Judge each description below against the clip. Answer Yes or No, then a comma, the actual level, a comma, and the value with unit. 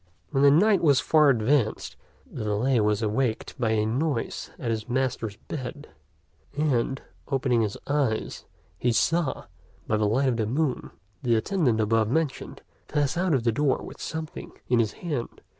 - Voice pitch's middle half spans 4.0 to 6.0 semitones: Yes, average, 4.8 semitones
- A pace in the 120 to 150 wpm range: No, average, 165 wpm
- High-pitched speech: No, low, 125 Hz